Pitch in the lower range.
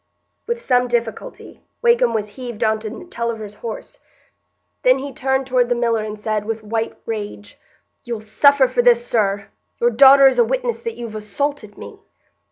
No: high, 235 Hz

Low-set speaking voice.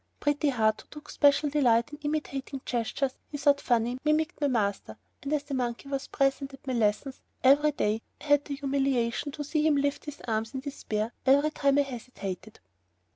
No: very high, 275 Hz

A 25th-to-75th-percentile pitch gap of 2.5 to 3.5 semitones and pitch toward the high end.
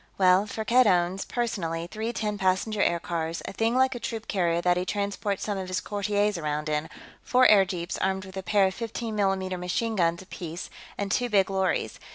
Yes: average, 3.1 semitones; high, 195 Hz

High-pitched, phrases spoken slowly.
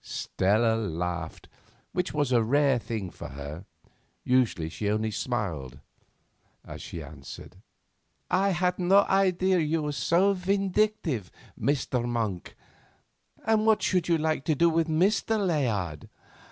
No: medium, 140 Hz; slow, 125 wpm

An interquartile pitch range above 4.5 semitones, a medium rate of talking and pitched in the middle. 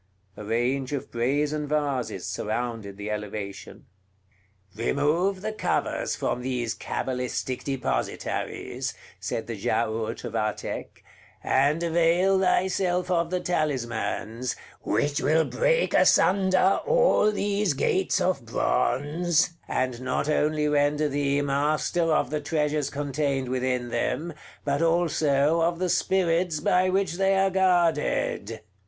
No: wide, 5.6 semitones; slow, 120 wpm; medium, 150 Hz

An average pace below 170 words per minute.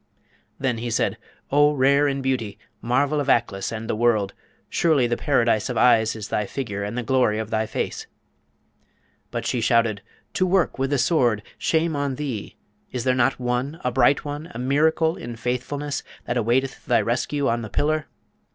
No: average, 180 wpm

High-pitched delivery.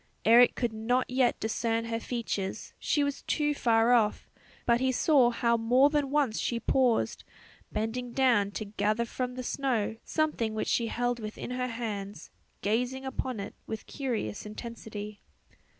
Yes: high, 235 Hz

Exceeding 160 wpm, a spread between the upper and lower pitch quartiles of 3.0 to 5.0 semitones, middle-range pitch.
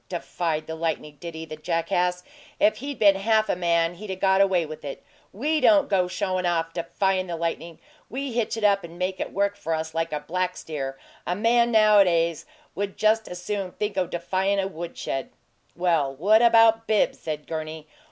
Yes: average, 200 wpm; average, 3.8 semitones; medium, 180 Hz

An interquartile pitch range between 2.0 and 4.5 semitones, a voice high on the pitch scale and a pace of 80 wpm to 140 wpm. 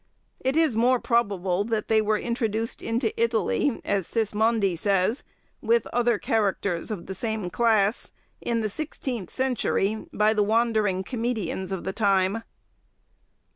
Yes: average, 2.9 semitones; high, 220 Hz; slow, 135 wpm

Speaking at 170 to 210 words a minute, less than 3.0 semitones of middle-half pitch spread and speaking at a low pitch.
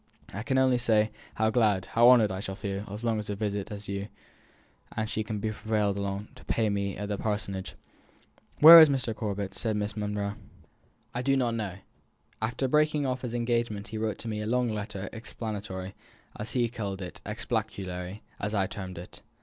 Yes: average, 190 wpm; narrow, 2.6 semitones; low, 105 Hz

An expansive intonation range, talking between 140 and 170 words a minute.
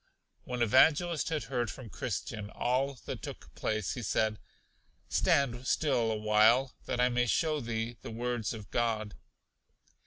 No: average, 3.0 semitones; average, 150 wpm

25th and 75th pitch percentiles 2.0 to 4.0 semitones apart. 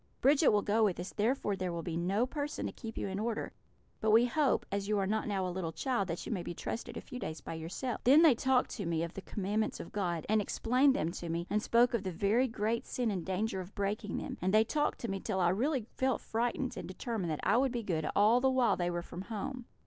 No: average, 4.6 semitones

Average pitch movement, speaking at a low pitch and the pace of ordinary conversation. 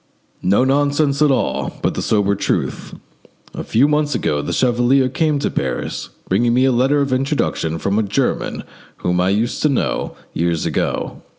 No: wide, 5.8 semitones; low, 125 Hz; average, 175 wpm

